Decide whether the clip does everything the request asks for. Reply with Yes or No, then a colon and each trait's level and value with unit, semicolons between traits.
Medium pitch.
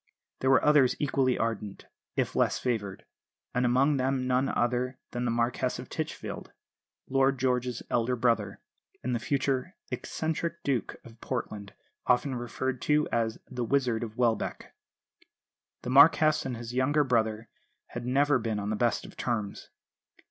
No: low, 125 Hz